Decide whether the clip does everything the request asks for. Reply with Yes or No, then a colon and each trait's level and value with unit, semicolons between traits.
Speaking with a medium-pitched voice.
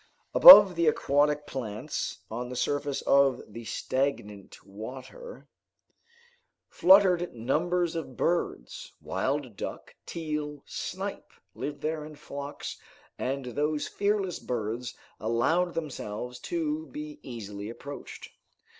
Yes: medium, 145 Hz